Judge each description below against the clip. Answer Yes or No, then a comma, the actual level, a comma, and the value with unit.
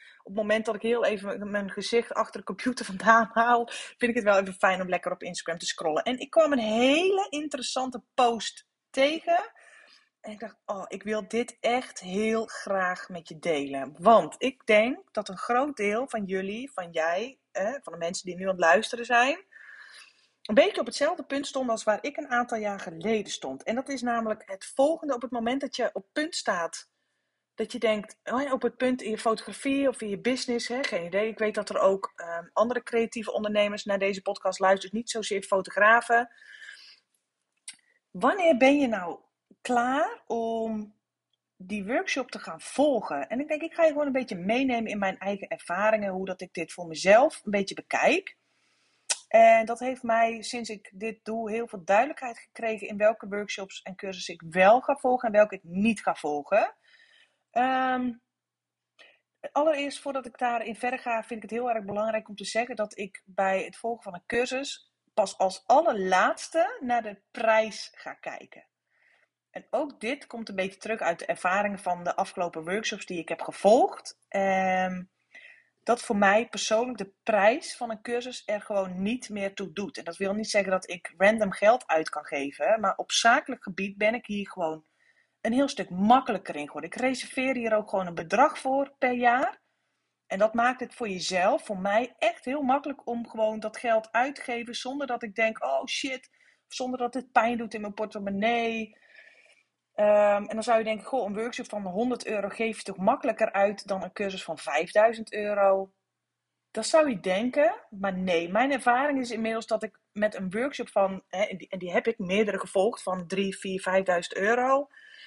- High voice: Yes, high, 225 Hz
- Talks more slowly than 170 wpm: No, average, 195 wpm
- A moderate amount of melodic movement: Yes, average, 4.3 semitones